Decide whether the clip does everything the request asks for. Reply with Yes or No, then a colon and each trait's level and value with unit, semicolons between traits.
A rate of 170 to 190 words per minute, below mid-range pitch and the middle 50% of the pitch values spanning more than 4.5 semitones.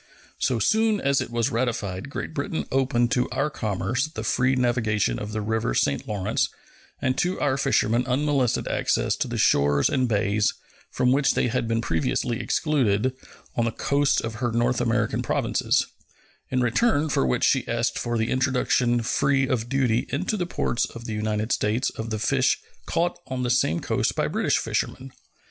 No: average, 180 wpm; low, 120 Hz; average, 3.4 semitones